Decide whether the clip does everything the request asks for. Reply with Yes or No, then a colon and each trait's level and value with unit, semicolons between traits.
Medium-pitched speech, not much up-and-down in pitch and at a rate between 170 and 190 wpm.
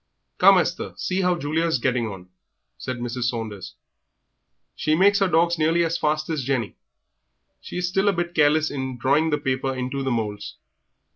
No: medium, 145 Hz; average, 5.1 semitones; average, 175 wpm